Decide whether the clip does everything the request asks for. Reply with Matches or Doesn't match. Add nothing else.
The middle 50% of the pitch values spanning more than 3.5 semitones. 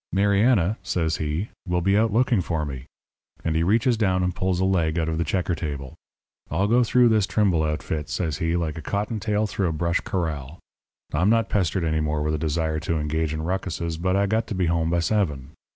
Matches